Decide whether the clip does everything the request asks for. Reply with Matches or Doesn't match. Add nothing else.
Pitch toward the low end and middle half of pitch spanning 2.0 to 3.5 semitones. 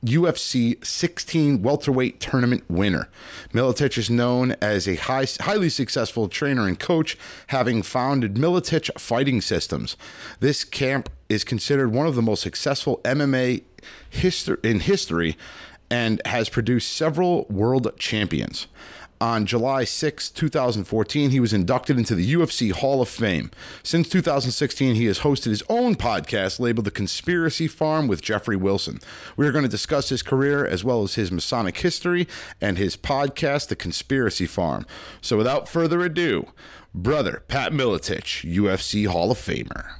Doesn't match